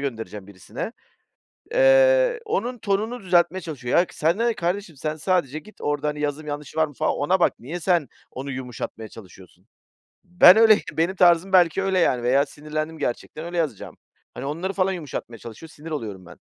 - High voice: No, medium, 160 Hz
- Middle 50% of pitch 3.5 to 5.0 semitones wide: No, wide, 5.4 semitones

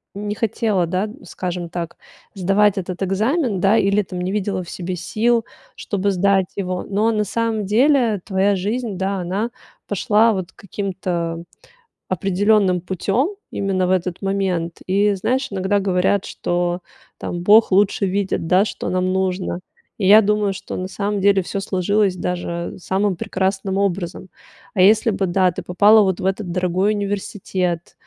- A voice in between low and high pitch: No, high, 195 Hz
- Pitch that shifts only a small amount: Yes, narrow, 2.1 semitones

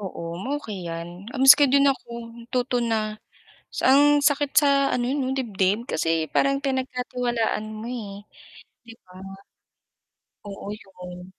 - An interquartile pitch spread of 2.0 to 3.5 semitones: No, average, 5.0 semitones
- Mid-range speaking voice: No, high, 235 Hz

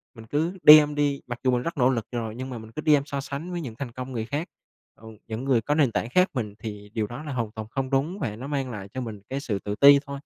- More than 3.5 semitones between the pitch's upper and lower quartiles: Yes, average, 4.3 semitones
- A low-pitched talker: Yes, low, 130 Hz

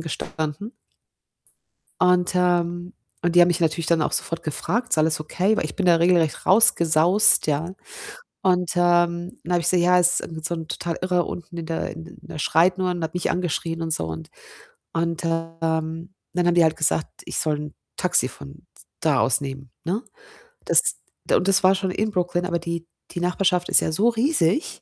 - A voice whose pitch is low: No, medium, 170 Hz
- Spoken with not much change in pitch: Yes, narrow, 2.0 semitones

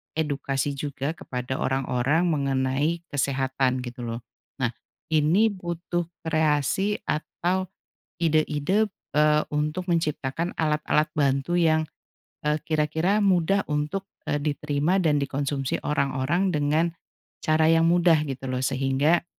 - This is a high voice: No, medium, 150 Hz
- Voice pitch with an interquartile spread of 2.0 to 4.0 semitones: Yes, average, 3.5 semitones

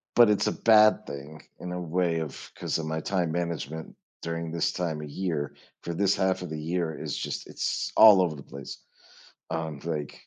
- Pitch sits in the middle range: No, very low, 85 Hz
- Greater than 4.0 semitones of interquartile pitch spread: No, average, 2.7 semitones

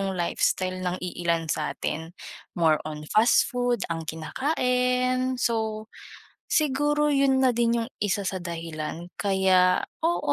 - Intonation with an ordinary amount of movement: No, wide, 6.5 semitones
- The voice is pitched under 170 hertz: No, high, 200 Hz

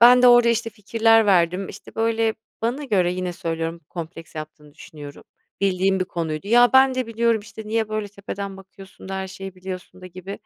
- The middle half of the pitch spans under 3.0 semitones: No, average, 3.8 semitones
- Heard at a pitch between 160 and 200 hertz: Yes, high, 195 Hz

